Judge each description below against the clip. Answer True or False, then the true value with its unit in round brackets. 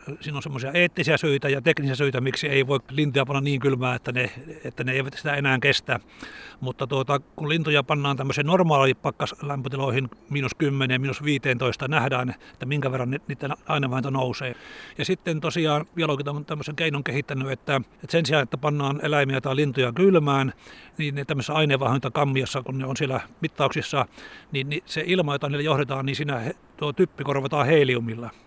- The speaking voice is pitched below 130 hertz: False (140 Hz)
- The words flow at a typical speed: False (170 wpm)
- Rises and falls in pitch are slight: True (2.2 semitones)